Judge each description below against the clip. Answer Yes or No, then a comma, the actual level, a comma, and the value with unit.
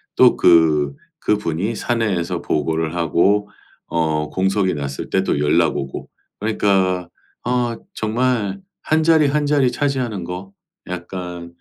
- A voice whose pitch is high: No, very low, 95 Hz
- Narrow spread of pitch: No, average, 5.2 semitones